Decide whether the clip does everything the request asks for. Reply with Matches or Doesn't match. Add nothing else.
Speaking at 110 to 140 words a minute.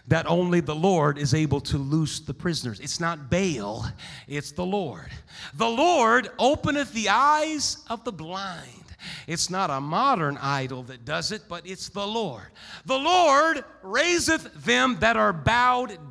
Doesn't match